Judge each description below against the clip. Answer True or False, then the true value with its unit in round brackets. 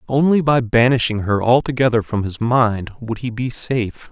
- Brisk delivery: False (175 wpm)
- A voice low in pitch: True (120 Hz)